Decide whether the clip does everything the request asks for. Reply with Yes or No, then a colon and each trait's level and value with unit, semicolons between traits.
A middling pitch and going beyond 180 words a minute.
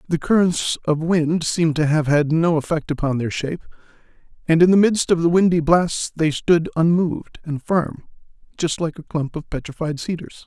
Yes: medium, 160 Hz; average, 190 wpm